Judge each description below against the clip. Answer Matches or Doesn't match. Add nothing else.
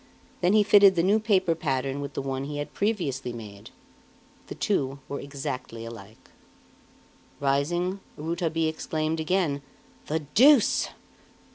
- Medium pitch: Matches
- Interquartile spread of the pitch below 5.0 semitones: Doesn't match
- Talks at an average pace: Doesn't match